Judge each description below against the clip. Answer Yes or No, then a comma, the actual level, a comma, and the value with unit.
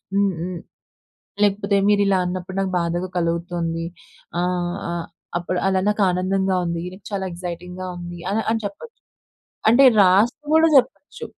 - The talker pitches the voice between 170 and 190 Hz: Yes, medium, 185 Hz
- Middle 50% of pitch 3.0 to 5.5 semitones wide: No, narrow, 2.4 semitones